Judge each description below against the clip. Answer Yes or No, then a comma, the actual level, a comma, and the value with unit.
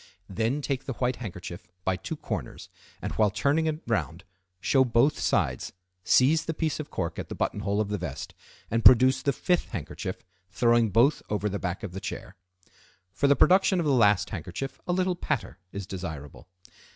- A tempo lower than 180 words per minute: No, average, 185 wpm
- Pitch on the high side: No, low, 115 Hz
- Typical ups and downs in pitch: No, wide, 6.8 semitones